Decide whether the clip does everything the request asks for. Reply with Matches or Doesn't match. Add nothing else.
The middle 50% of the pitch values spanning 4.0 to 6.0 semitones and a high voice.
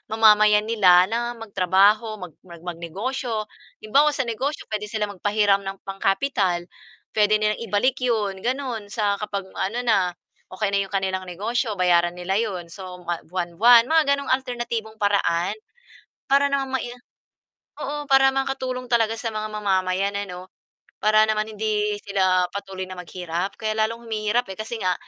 Doesn't match